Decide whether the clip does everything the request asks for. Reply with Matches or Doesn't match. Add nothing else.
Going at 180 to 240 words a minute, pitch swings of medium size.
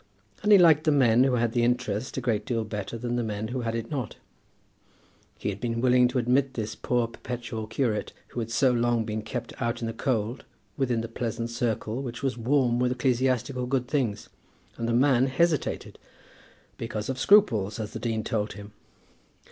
Doesn't match